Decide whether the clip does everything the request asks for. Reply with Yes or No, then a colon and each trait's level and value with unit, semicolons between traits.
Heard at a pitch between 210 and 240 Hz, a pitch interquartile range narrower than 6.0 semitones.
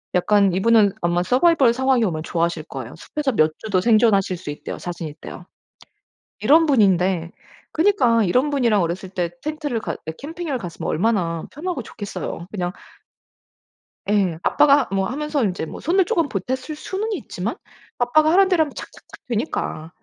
No: high, 220 Hz; wide, 8.5 semitones